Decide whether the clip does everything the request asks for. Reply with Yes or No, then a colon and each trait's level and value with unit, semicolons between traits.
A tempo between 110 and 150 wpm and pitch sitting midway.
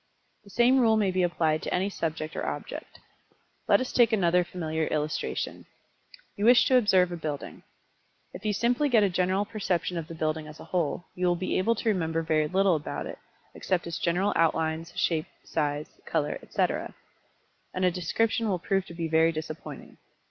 No: average, 185 wpm; medium, 175 Hz